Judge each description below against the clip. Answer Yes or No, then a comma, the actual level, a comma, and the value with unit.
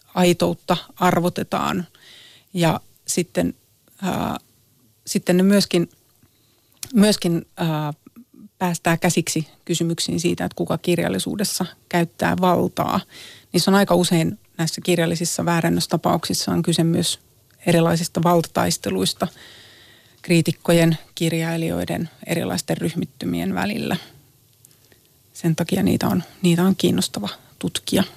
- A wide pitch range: Yes, wide, 6.1 semitones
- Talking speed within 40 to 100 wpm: Yes, slow, 95 wpm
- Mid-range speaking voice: Yes, medium, 170 Hz